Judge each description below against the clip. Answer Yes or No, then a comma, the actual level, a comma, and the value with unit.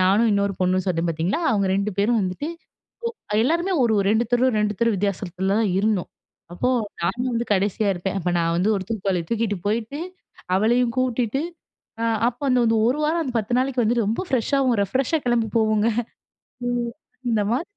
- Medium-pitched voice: No, high, 220 Hz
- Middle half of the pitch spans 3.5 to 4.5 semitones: Yes, average, 3.8 semitones